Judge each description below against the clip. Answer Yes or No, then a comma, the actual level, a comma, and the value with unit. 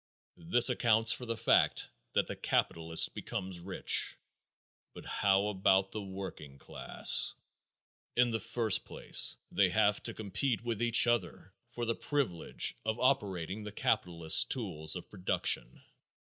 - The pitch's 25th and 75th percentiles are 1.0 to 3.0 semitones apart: No, average, 4.5 semitones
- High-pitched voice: No, low, 100 Hz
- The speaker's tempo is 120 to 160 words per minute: Yes, slow, 135 wpm